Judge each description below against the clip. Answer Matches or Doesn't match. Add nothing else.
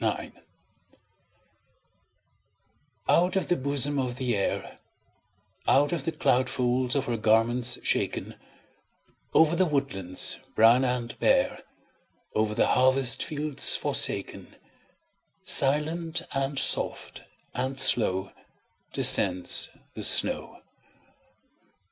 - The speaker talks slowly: Matches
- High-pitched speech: Doesn't match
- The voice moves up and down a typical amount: Matches